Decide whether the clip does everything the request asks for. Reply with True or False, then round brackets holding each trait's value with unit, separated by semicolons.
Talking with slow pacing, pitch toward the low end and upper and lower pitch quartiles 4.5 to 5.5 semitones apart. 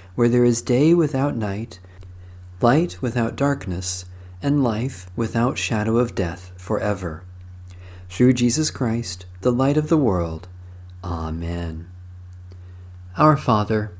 True (115 wpm; 95 Hz; 5.2 semitones)